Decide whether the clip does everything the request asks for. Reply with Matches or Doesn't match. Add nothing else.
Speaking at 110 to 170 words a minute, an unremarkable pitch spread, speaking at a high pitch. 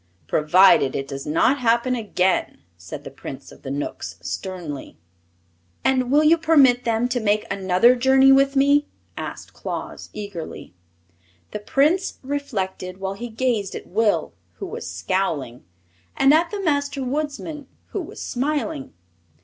Doesn't match